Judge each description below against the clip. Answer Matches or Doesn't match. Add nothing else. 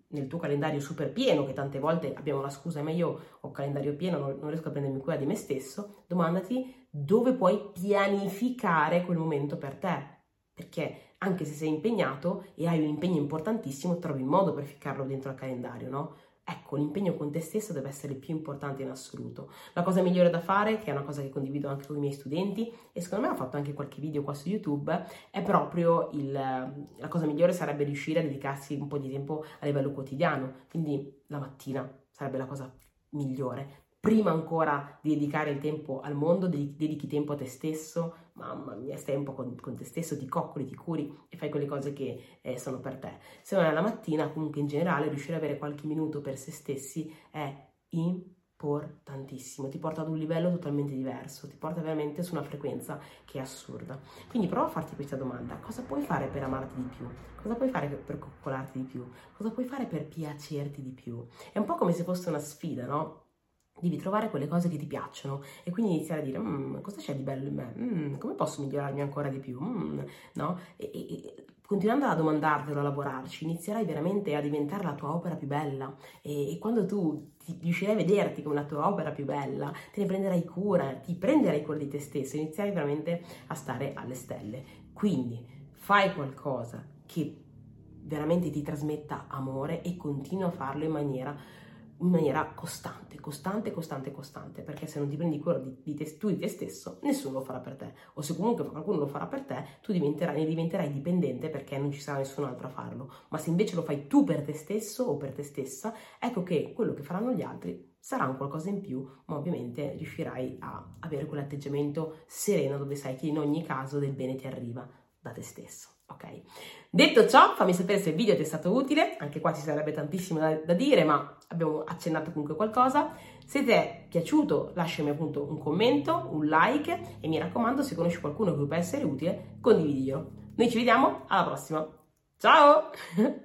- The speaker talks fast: Matches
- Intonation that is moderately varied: Matches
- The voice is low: Doesn't match